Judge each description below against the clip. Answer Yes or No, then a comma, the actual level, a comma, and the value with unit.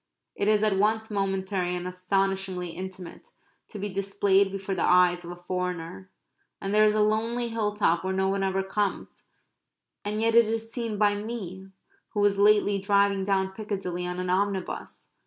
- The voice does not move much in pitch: Yes, narrow, 2.0 semitones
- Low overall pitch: No, high, 195 Hz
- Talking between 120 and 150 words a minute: No, average, 175 wpm